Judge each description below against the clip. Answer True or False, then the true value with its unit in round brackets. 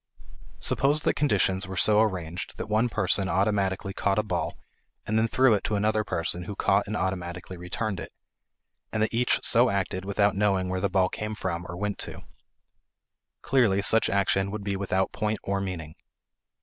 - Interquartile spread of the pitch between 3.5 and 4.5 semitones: False (2.4 semitones)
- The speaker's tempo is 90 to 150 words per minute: False (180 wpm)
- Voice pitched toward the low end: True (100 Hz)